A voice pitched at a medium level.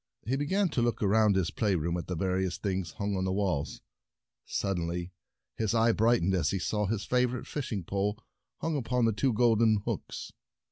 No: low, 105 Hz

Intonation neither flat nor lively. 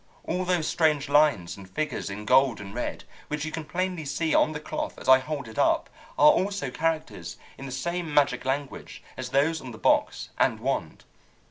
Yes: average, 3.5 semitones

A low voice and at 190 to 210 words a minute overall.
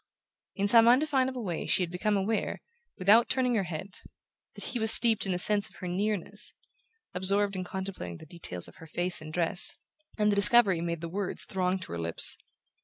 No: high, 195 Hz; average, 195 wpm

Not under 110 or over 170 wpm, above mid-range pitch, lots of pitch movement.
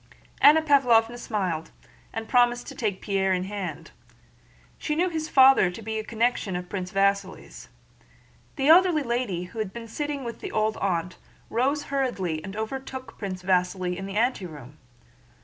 Yes: average, 160 wpm; high, 220 Hz; wide, 5.7 semitones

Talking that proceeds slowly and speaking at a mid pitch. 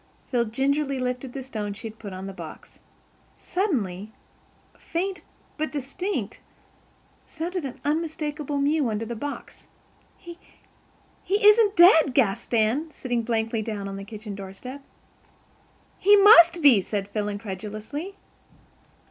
No: slow, 125 wpm; very high, 255 Hz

